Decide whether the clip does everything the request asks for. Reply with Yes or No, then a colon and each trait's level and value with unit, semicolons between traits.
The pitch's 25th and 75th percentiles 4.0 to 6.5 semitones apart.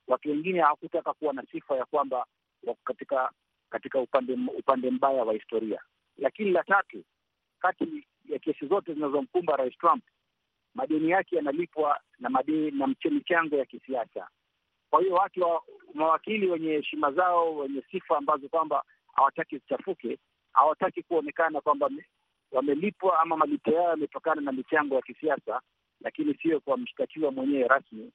Yes: average, 4.6 semitones